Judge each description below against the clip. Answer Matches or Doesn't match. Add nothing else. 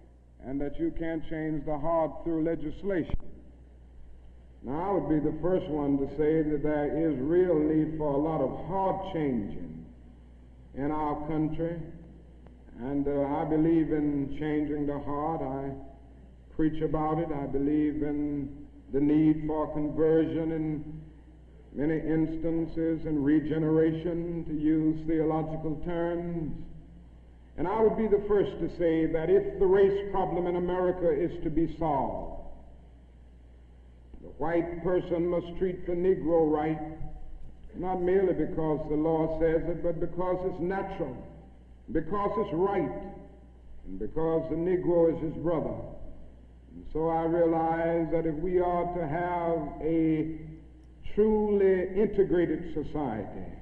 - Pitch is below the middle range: Doesn't match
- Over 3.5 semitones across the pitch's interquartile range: Doesn't match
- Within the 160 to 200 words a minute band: Doesn't match